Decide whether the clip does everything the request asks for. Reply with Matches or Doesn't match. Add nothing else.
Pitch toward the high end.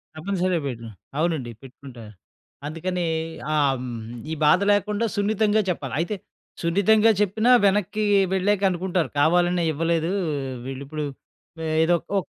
Doesn't match